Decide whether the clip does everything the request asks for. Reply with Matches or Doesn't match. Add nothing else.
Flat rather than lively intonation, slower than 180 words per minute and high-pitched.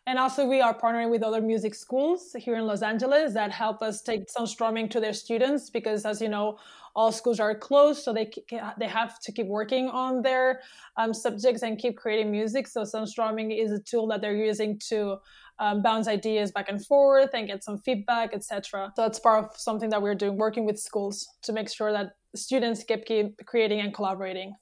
Doesn't match